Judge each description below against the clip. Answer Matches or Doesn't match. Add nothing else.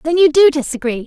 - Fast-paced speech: Matches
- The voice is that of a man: Doesn't match